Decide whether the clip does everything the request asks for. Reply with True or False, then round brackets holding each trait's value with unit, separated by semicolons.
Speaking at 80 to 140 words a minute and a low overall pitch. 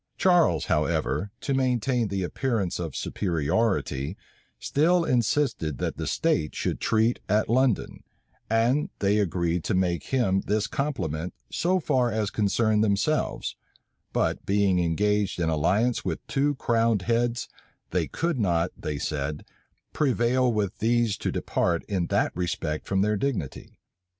True (135 wpm; 105 Hz)